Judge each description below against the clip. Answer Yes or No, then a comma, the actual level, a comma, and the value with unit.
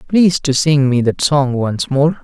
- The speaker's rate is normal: No, fast, 215 wpm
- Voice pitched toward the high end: No, medium, 140 Hz